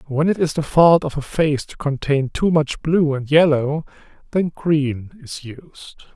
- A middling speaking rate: Yes, average, 185 wpm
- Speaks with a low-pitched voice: No, medium, 150 Hz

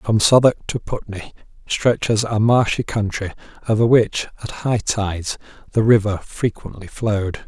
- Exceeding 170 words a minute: No, slow, 135 wpm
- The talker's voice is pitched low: Yes, low, 110 Hz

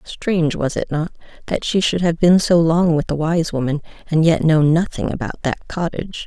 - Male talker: No, female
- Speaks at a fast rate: Yes, fast, 210 wpm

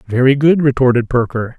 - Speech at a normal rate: Yes, average, 150 wpm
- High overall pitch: No, low, 130 Hz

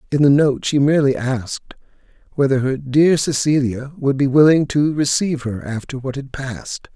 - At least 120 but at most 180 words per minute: Yes, average, 170 wpm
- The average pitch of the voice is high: No, medium, 140 Hz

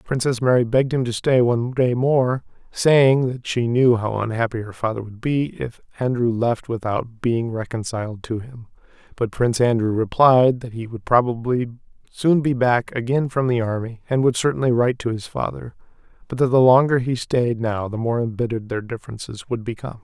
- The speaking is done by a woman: No, male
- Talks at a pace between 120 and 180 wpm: No, average, 190 wpm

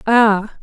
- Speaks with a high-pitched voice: Yes, high, 215 Hz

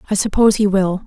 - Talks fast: Yes, fast, 225 wpm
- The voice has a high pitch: Yes, high, 200 Hz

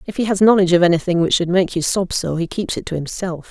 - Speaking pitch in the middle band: Yes, medium, 180 Hz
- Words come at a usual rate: No, fast, 290 wpm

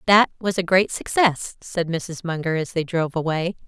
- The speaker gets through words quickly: No, average, 195 wpm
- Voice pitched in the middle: Yes, medium, 175 Hz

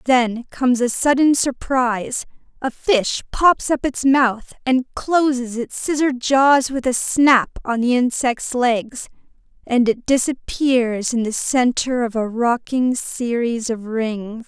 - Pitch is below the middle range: No, very high, 250 Hz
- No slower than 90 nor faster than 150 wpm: Yes, average, 145 wpm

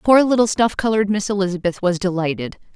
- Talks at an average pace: Yes, average, 175 wpm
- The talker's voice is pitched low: No, high, 200 Hz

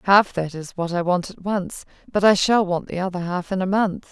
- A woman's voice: Yes, female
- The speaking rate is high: Yes, fast, 260 wpm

